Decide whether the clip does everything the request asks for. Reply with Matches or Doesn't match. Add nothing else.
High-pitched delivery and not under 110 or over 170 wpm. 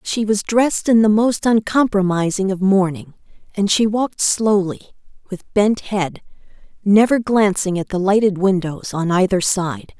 Matches